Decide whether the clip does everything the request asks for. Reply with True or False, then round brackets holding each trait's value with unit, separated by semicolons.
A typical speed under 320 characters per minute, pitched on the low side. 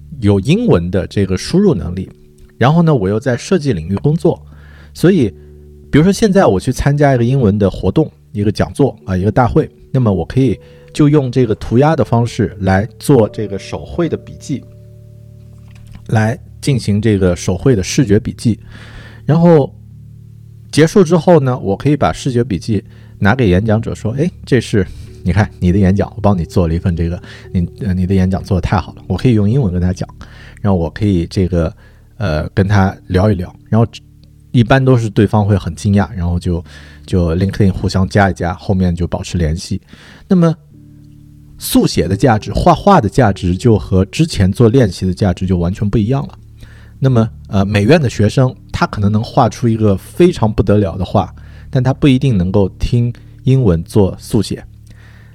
True (280 characters per minute; 105 Hz)